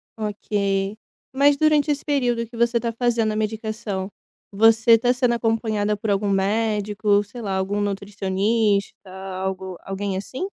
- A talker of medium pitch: No, high, 215 Hz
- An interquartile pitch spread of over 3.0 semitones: No, average, 2.7 semitones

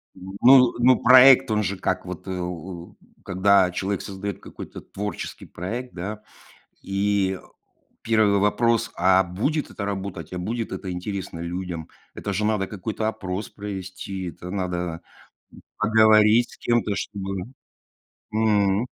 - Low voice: Yes, low, 100 Hz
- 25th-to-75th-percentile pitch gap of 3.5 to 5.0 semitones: No, average, 2.7 semitones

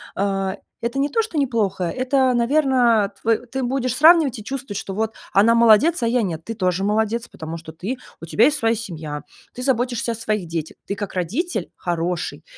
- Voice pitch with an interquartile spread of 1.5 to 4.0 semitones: No, average, 4.8 semitones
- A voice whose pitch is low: No, high, 225 Hz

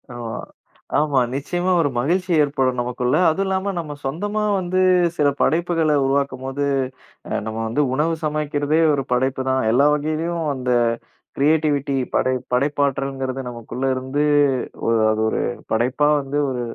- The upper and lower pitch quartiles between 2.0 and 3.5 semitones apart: Yes, average, 3.2 semitones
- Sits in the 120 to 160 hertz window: Yes, medium, 140 Hz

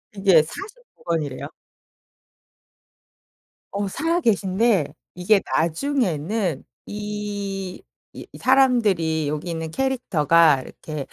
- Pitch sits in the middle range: No, high, 195 Hz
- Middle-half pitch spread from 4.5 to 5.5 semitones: No, wide, 5.9 semitones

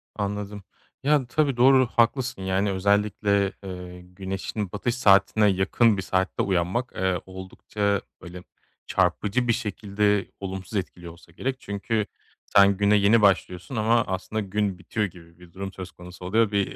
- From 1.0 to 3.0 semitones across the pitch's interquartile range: Yes, narrow, 2.4 semitones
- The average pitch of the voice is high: No, low, 100 Hz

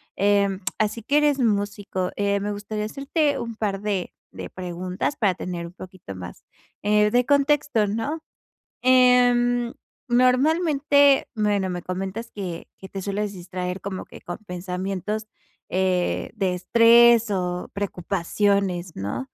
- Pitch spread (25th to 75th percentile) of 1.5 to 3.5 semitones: No, average, 4.6 semitones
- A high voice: Yes, high, 205 Hz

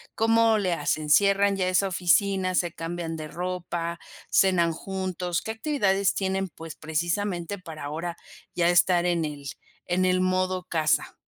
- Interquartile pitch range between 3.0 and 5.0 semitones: No, narrow, 2.4 semitones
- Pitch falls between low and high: Yes, medium, 180 Hz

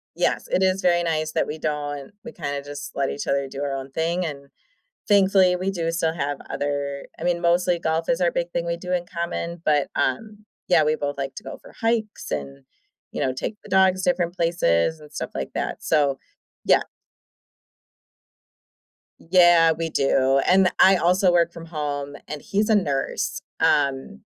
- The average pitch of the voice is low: No, medium, 165 Hz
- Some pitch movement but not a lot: Yes, average, 4.0 semitones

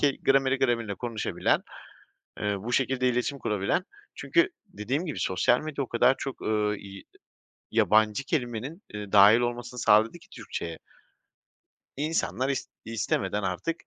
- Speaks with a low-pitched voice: Yes, low, 120 Hz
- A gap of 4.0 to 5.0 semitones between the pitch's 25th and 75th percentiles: Yes, average, 4.5 semitones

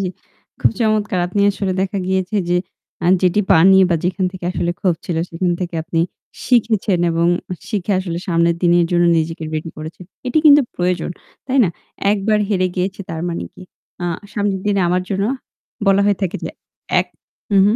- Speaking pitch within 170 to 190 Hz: Yes, medium, 185 Hz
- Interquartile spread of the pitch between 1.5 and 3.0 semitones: Yes, average, 2.7 semitones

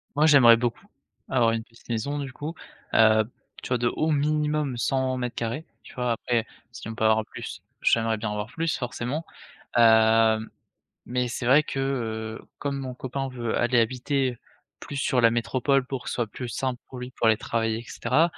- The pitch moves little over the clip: No, average, 3.0 semitones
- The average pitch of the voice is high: No, low, 125 Hz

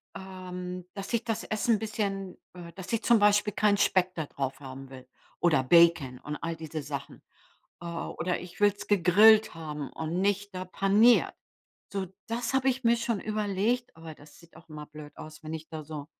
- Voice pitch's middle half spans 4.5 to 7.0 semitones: Yes, average, 4.9 semitones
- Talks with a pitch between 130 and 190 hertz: Yes, medium, 185 Hz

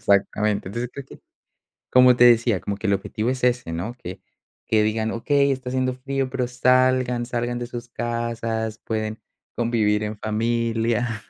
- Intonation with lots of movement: No, narrow, 2.4 semitones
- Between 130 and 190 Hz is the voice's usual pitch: No, low, 120 Hz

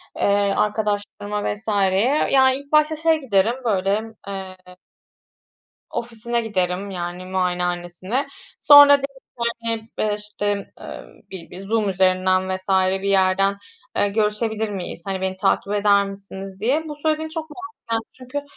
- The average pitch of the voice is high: Yes, high, 205 Hz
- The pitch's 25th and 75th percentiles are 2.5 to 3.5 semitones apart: No, average, 4.0 semitones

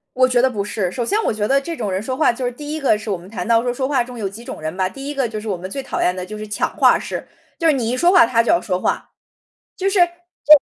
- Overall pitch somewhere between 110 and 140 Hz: No, high, 240 Hz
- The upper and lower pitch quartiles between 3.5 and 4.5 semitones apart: No, average, 4.9 semitones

